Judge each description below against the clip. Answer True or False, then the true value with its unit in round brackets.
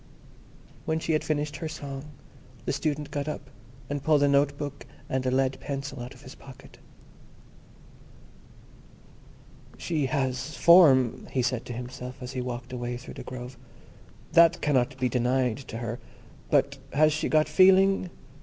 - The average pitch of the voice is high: False (135 Hz)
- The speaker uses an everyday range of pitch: True (3.2 semitones)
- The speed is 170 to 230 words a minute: False (155 wpm)